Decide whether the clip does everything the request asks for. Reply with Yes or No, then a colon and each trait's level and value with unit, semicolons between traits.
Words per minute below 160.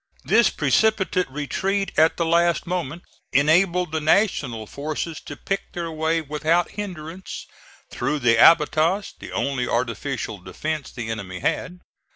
Yes: slow, 135 wpm